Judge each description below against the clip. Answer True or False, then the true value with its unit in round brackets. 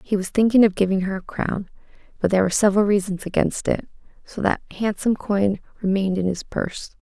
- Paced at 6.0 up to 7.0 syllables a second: True (6.4 syllables/s)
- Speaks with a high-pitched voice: True (195 Hz)